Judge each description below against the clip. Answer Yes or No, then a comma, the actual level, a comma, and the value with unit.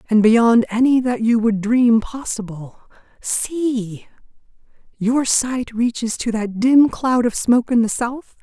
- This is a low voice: No, high, 235 Hz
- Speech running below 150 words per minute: Yes, average, 140 wpm